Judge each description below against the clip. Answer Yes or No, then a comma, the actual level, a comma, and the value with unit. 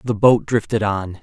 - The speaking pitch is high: No, low, 105 Hz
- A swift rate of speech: No, average, 195 wpm